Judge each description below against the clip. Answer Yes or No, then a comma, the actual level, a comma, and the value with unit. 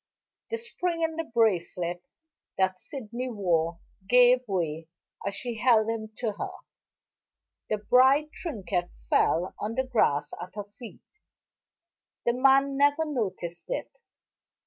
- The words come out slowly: Yes, slow, 125 wpm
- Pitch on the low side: No, high, 225 Hz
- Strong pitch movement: Yes, wide, 6.4 semitones